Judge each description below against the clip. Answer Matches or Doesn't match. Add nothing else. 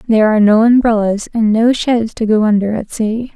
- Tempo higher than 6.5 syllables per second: Doesn't match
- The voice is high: Matches